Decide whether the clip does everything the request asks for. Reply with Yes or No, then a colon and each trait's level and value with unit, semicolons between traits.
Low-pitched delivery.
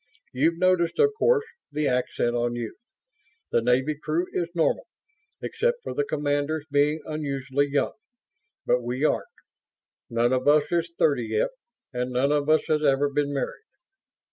No: medium, 145 Hz